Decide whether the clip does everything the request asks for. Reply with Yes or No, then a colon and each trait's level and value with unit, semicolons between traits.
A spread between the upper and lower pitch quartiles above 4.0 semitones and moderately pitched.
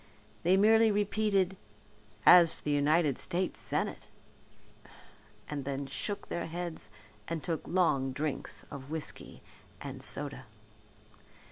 Yes: average, 4.9 semitones; medium, 160 Hz